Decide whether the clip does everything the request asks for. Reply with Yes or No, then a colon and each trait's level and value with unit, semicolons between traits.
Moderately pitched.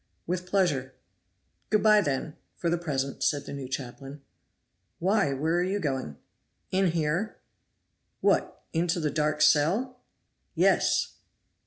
Yes: medium, 160 Hz